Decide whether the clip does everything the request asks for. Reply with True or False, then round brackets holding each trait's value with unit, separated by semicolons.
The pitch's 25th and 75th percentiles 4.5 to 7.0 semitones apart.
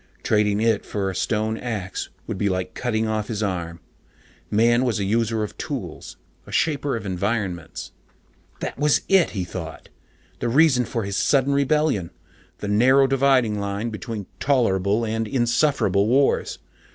False (4.1 semitones)